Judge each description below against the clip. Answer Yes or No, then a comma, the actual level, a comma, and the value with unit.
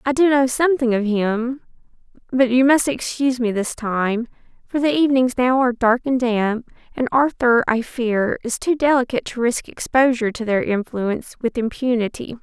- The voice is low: No, high, 245 Hz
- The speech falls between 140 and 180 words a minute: Yes, average, 170 wpm